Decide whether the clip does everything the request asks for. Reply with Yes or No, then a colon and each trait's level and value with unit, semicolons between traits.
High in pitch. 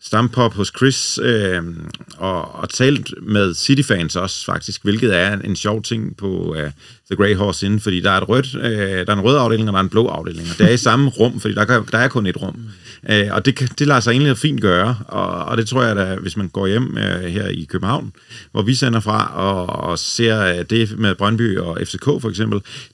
No: low, 105 Hz